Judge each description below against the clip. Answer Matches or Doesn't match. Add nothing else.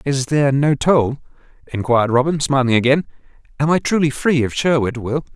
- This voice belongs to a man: Matches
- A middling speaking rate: Matches